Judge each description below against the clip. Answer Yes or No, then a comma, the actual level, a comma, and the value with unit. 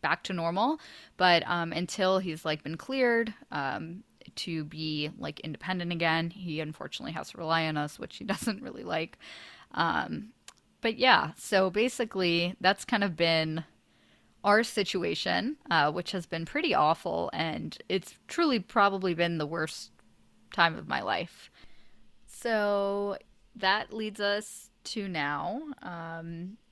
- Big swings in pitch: No, average, 4.8 semitones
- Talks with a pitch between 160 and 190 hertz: Yes, medium, 185 Hz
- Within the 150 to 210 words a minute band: No, average, 140 wpm